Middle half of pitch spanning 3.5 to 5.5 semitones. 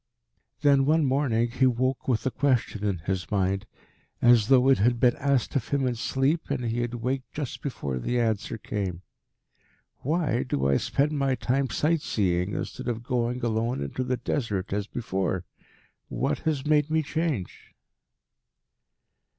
Yes: average, 4.5 semitones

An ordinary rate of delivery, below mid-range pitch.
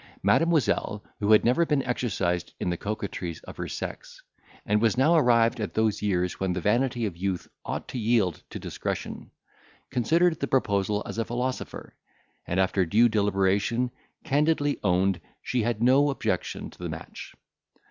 Yes: average, 160 wpm; low, 110 Hz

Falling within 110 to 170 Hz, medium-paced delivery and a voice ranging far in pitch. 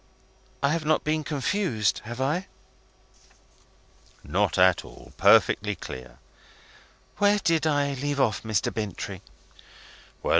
No: medium, 140 Hz; slow, 110 wpm; wide, 6.4 semitones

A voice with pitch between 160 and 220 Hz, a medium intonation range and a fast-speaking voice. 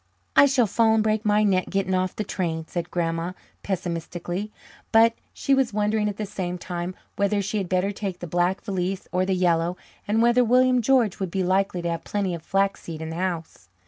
Yes: high, 190 Hz; average, 3.3 semitones; fast, 210 wpm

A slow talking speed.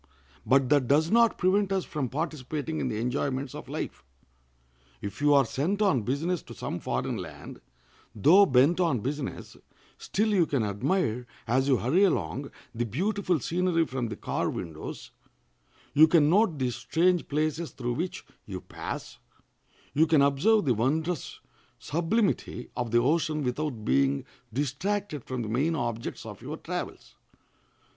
No: average, 150 wpm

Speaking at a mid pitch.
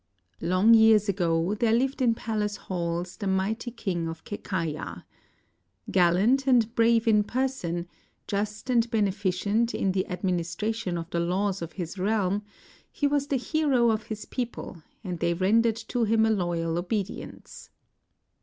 No: high, 205 Hz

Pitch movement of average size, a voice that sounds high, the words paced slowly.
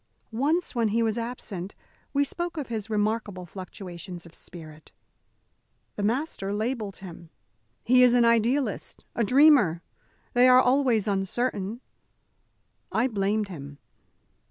Yes: average, 4.5 semitones; high, 220 Hz; slow, 125 wpm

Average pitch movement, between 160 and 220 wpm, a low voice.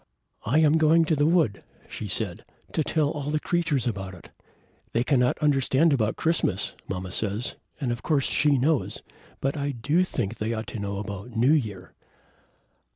No: wide, 6.1 semitones; average, 175 wpm; low, 130 Hz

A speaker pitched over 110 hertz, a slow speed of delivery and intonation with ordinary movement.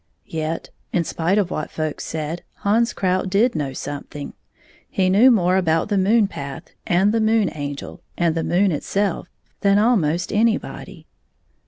No: medium, 185 Hz; average, 155 wpm; average, 4.5 semitones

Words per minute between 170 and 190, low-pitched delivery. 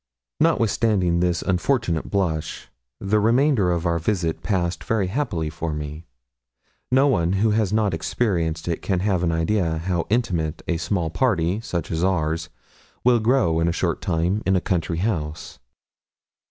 No: average, 155 wpm; very low, 90 Hz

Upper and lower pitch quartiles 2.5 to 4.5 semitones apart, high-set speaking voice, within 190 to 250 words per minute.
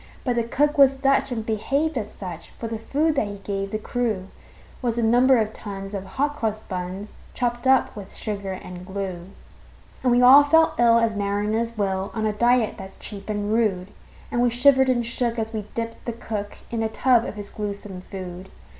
Yes: average, 3.4 semitones; high, 220 Hz; fast, 205 wpm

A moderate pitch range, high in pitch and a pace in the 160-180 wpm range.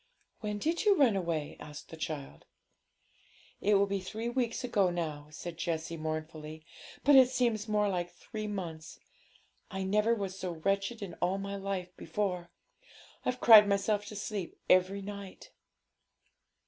No: average, 3.7 semitones; high, 195 Hz; average, 150 wpm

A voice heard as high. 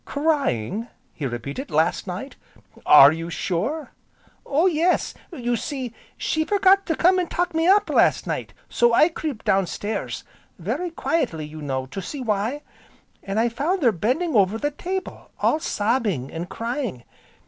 Yes: high, 240 Hz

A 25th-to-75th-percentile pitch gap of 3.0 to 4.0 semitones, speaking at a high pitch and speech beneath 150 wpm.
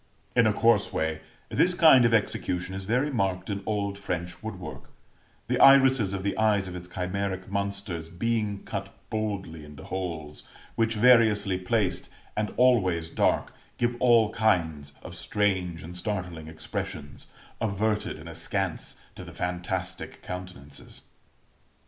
No: average, 3.6 semitones; low, 100 Hz; slow, 135 wpm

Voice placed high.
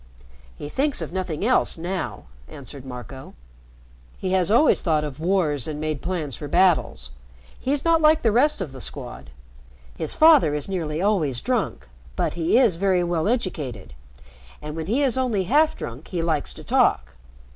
No: medium, 170 Hz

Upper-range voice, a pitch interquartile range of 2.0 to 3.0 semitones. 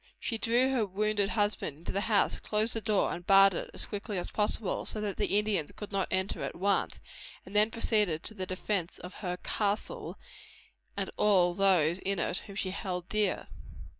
Yes: high, 200 Hz; narrow, 2.4 semitones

